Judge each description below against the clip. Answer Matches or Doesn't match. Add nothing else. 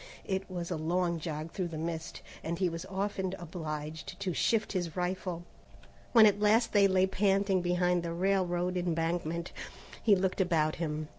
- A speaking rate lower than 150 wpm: Doesn't match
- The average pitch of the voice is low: Doesn't match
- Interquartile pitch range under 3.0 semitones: Matches